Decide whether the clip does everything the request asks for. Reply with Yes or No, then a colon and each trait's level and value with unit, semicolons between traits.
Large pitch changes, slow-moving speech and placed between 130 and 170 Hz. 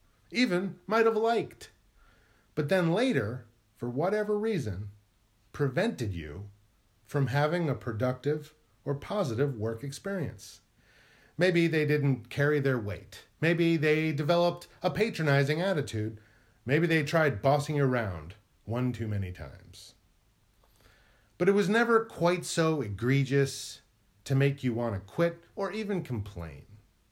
Yes: wide, 7.4 semitones; slow, 130 wpm; medium, 140 Hz